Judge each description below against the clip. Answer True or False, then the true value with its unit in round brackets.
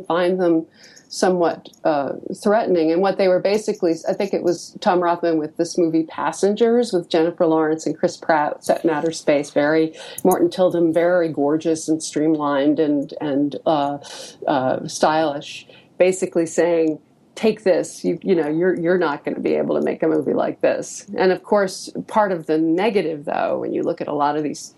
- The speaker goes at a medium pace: True (185 wpm)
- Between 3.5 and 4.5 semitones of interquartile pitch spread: False (2.6 semitones)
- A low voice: False (170 Hz)